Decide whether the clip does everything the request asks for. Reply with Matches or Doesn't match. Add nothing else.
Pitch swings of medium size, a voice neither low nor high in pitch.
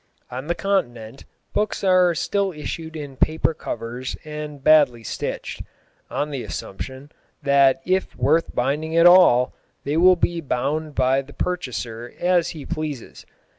Matches